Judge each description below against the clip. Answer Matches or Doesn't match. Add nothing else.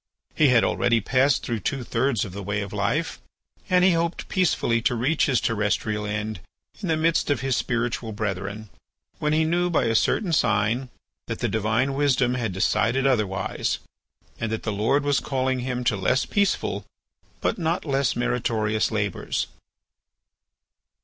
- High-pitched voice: Doesn't match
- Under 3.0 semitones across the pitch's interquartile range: Doesn't match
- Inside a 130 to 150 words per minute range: Doesn't match